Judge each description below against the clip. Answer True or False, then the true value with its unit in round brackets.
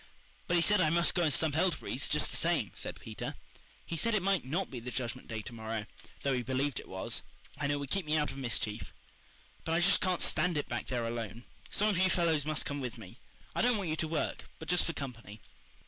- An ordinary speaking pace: False (245 wpm)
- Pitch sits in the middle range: True (150 Hz)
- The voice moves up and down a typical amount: False (6.2 semitones)